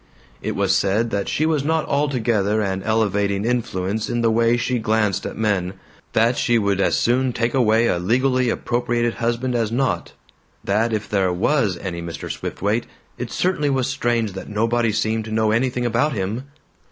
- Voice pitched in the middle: No, low, 115 Hz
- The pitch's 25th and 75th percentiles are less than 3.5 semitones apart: Yes, average, 3.1 semitones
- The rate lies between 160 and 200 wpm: Yes, average, 175 wpm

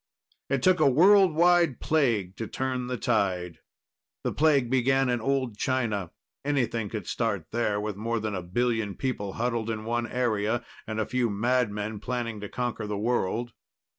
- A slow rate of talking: No, average, 165 wpm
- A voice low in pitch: Yes, low, 115 Hz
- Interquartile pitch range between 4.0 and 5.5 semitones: No, average, 3.5 semitones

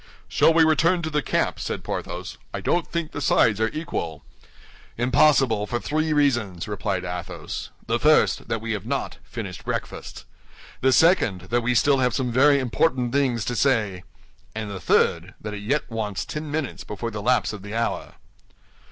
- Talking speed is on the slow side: No, average, 180 wpm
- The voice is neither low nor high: No, low, 120 Hz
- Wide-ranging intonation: Yes, wide, 5.7 semitones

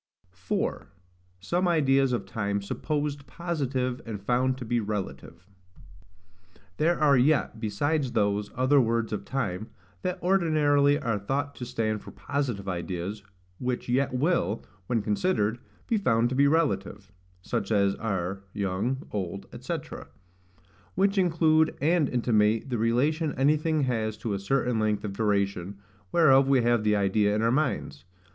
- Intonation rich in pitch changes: Yes, wide, 5.8 semitones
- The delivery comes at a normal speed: Yes, average, 145 wpm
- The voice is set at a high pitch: No, low, 120 Hz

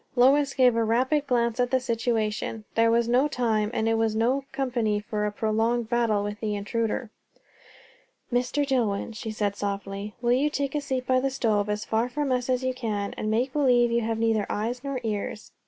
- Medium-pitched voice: No, high, 235 Hz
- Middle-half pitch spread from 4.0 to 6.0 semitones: No, average, 2.9 semitones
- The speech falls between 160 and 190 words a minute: No, fast, 205 wpm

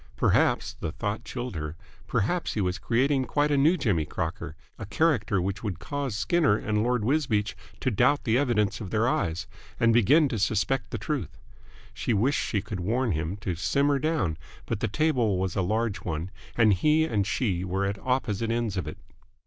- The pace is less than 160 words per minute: No, average, 190 wpm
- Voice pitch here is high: No, low, 110 Hz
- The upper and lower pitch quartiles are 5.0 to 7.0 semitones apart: Yes, average, 5.3 semitones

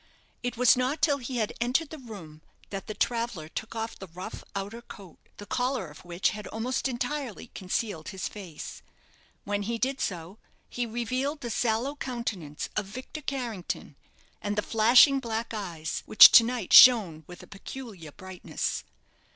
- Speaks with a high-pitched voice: Yes, high, 225 Hz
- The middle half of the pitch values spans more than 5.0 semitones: No, average, 4.6 semitones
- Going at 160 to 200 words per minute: Yes, average, 165 wpm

